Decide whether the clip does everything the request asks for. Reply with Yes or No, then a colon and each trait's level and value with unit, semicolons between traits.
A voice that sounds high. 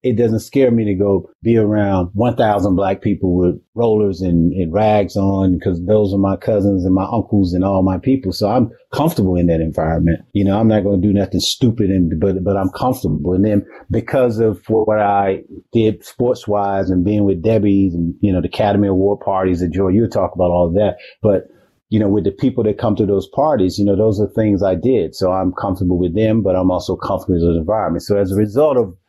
No: low, 100 Hz